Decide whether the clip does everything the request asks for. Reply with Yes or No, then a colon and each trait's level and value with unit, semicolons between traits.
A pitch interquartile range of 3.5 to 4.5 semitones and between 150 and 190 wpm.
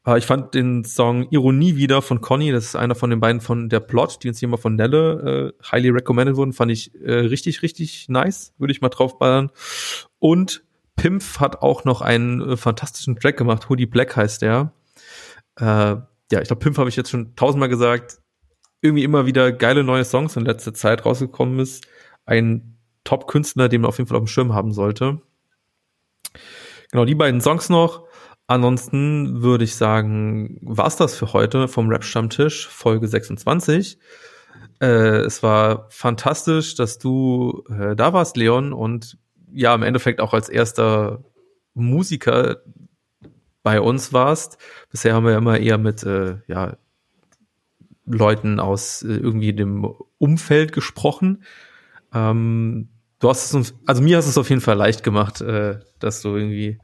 Yes: average, 3.8 semitones; average, 165 wpm